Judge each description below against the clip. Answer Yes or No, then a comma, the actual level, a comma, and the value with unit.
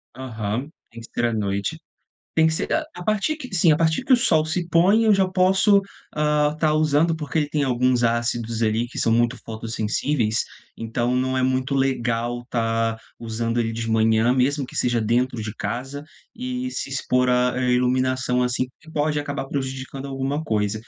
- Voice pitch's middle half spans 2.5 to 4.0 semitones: No, average, 4.7 semitones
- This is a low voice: Yes, low, 130 Hz